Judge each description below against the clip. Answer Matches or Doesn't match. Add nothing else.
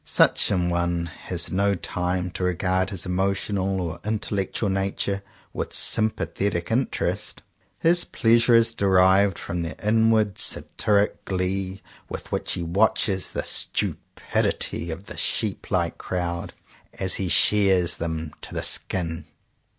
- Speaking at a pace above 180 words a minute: Doesn't match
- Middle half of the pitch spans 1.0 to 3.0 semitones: Matches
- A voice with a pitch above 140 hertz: Doesn't match